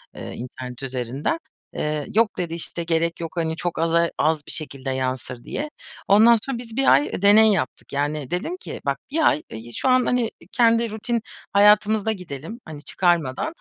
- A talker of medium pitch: Yes, medium, 170 Hz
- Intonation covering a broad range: Yes, wide, 7.2 semitones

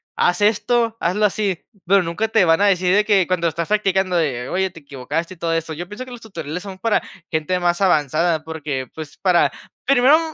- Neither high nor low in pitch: Yes, medium, 180 Hz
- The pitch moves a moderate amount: Yes, average, 4.0 semitones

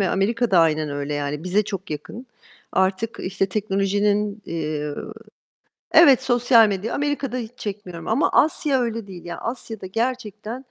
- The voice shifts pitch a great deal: No, average, 4.3 semitones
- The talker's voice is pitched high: Yes, high, 205 Hz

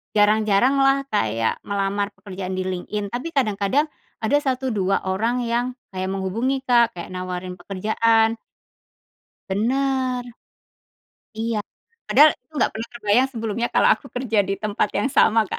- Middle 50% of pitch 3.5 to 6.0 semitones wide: Yes, average, 4.1 semitones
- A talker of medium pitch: No, high, 220 Hz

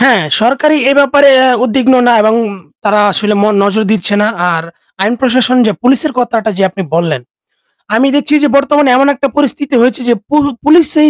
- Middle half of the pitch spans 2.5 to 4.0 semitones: No, average, 4.6 semitones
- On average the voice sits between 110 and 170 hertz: No, very high, 255 Hz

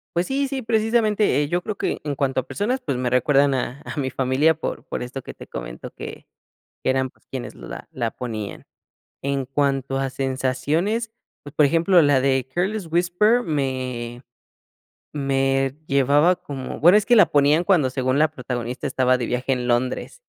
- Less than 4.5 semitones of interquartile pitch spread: No, average, 5.0 semitones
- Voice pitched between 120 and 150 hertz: Yes, medium, 140 Hz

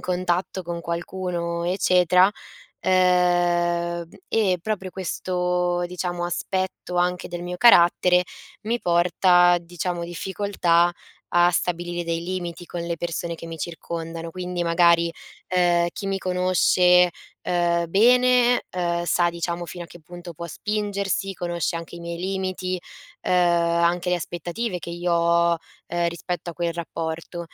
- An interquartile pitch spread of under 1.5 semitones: Yes, narrow, 1.1 semitones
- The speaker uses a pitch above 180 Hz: No, medium, 175 Hz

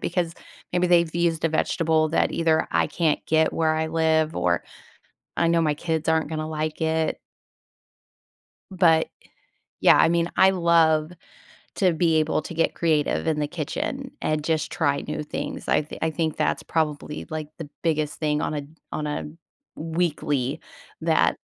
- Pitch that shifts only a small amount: Yes, narrow, 1.4 semitones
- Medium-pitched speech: Yes, medium, 160 Hz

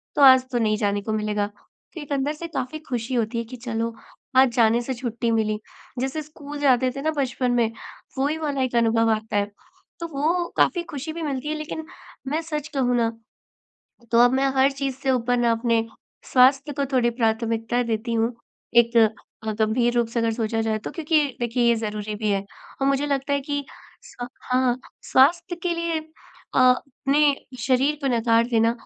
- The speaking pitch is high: Yes, very high, 250 Hz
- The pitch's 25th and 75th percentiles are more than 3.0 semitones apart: Yes, average, 3.7 semitones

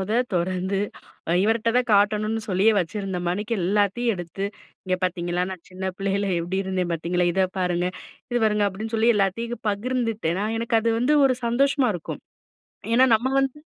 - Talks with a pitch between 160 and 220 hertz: Yes, high, 200 Hz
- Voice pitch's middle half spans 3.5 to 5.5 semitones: Yes, average, 4.0 semitones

